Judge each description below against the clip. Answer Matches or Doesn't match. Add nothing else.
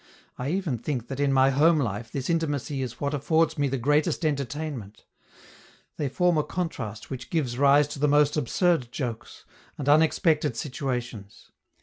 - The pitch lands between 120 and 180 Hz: Matches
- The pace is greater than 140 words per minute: Matches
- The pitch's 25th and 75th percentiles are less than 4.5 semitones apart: Matches